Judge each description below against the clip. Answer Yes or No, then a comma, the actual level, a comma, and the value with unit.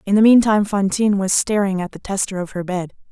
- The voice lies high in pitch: Yes, high, 200 Hz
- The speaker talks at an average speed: No, fast, 230 wpm